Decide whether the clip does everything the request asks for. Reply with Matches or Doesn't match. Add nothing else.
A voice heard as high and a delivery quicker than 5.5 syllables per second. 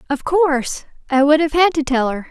Doesn't match